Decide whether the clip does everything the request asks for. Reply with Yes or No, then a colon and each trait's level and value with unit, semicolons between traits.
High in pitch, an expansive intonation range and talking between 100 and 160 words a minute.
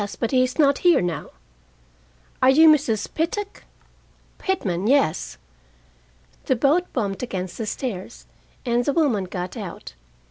Yes: very high, 250 Hz; wide, 7.2 semitones; slow, 135 wpm